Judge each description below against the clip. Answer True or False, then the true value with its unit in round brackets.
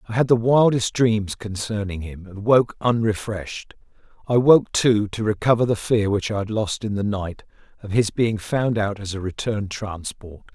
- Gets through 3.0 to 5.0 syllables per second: True (4.7 syllables/s)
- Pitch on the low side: True (105 Hz)